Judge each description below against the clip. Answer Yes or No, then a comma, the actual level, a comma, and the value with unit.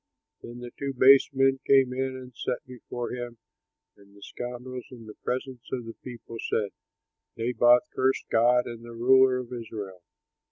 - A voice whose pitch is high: No, low, 125 Hz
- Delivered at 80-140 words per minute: No, average, 165 wpm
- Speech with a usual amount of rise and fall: No, narrow, 1.8 semitones